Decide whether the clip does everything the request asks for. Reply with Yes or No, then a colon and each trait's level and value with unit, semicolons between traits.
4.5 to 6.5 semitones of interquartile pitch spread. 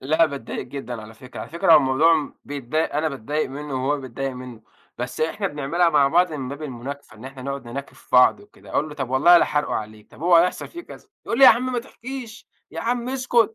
Yes: average, 5.0 semitones